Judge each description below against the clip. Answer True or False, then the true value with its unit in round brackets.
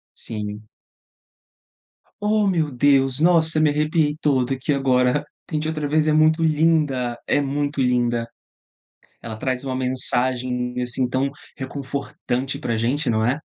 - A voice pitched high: False (135 Hz)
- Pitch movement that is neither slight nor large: True (3.5 semitones)